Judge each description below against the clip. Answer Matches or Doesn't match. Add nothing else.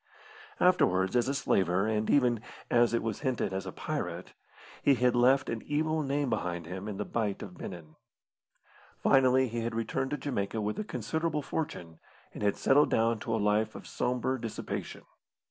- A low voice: Matches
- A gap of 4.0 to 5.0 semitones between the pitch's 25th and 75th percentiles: Matches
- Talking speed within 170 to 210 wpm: Matches